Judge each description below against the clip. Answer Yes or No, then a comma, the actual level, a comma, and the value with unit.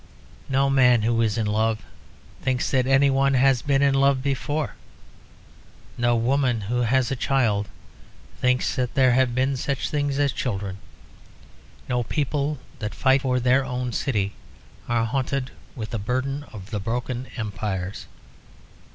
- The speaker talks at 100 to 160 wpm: Yes, average, 150 wpm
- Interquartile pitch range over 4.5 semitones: No, average, 3.0 semitones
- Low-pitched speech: Yes, low, 125 Hz